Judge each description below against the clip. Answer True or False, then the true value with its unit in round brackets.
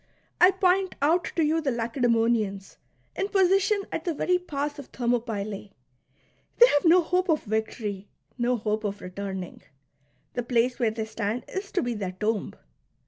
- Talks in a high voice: True (245 Hz)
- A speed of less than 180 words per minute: True (165 wpm)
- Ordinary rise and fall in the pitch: False (7.9 semitones)